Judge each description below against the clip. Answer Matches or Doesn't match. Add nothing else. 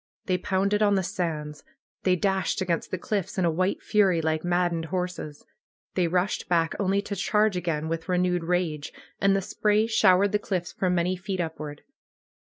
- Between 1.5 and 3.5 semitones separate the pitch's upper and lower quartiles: Matches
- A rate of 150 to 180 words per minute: Matches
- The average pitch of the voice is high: Doesn't match